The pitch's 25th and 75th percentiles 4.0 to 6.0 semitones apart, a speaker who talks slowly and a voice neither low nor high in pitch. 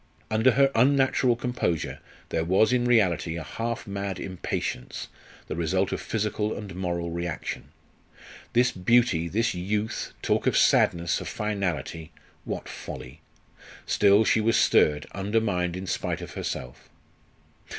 No: average, 4.8 semitones; slow, 130 wpm; low, 100 Hz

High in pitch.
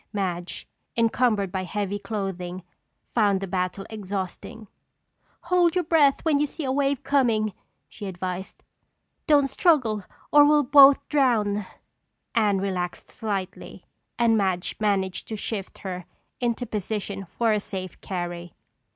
Yes: high, 210 Hz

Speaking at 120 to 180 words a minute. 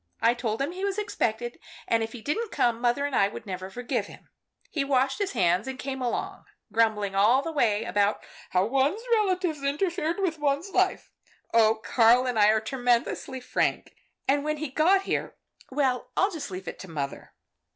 No: average, 195 wpm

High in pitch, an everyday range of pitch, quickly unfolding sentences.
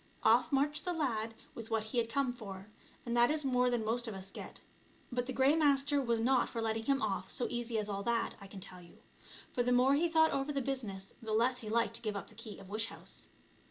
Yes: high, 235 Hz; average, 3.6 semitones; fast, 255 wpm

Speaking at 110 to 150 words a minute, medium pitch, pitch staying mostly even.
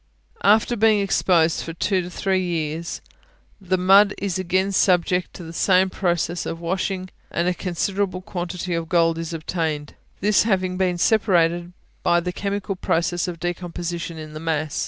No: average, 160 wpm; medium, 180 Hz; narrow, 2.1 semitones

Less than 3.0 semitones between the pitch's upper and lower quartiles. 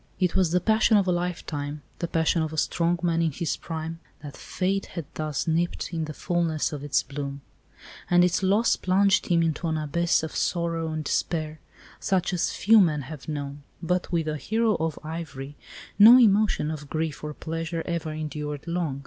Yes: narrow, 2.6 semitones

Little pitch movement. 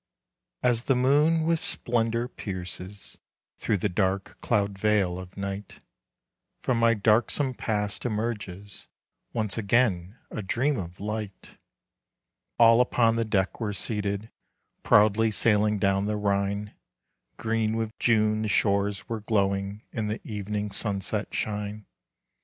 Yes: narrow, 2.3 semitones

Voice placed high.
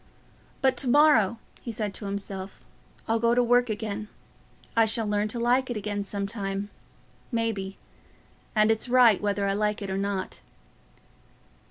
Yes: high, 215 Hz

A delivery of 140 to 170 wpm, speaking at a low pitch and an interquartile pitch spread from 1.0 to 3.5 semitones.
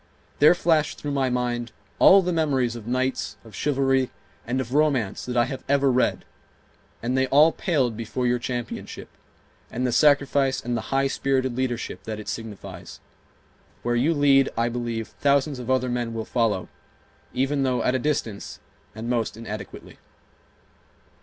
Yes: average, 160 wpm; low, 125 Hz; average, 2.7 semitones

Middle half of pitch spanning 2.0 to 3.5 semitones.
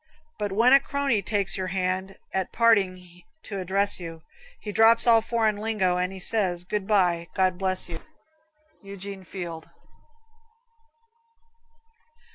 Yes: average, 2.8 semitones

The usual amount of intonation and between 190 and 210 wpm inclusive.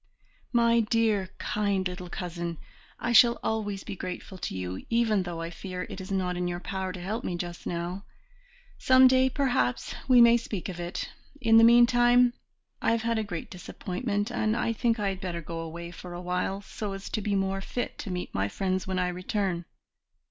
Yes: average, 4.3 semitones; average, 200 wpm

